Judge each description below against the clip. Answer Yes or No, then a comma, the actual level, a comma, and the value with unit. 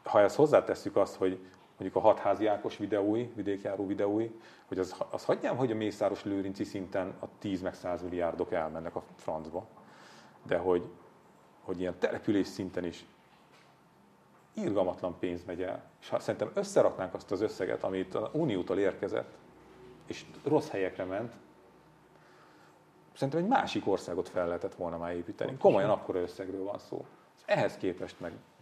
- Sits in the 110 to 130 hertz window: No, very low, 95 Hz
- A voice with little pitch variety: Yes, narrow, 2.2 semitones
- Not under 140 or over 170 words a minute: Yes, average, 150 wpm